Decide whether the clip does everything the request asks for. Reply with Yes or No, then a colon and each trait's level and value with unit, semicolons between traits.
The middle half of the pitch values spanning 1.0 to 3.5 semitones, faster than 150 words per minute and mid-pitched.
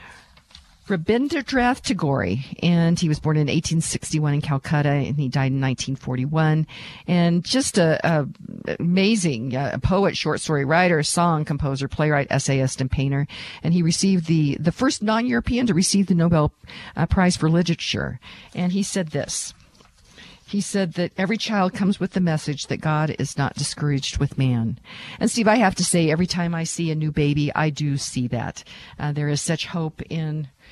No: average, 4.3 semitones; average, 175 wpm; medium, 160 Hz